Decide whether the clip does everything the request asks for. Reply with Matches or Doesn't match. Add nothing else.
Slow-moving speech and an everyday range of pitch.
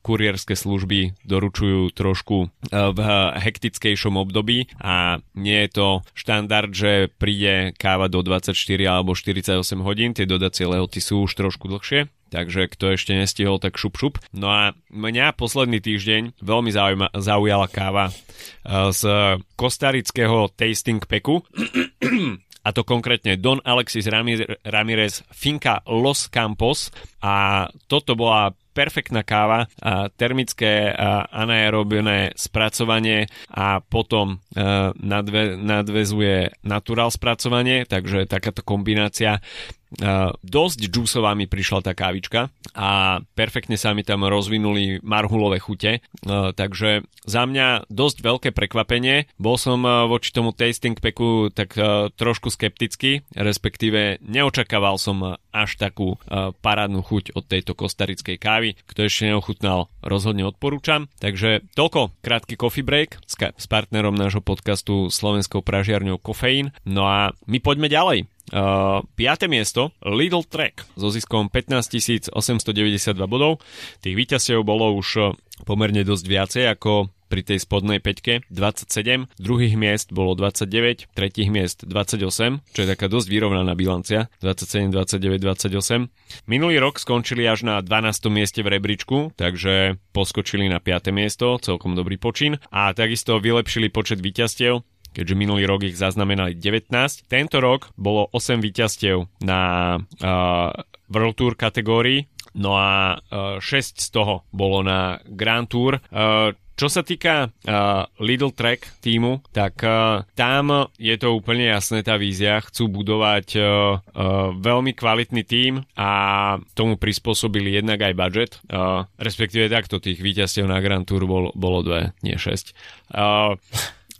Doesn't match